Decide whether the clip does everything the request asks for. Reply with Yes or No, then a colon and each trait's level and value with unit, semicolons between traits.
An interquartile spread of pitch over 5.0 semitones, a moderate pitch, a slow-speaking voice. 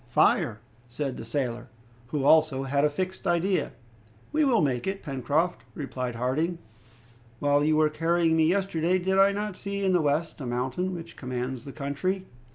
No: wide, 5.4 semitones; medium, 155 Hz; average, 170 wpm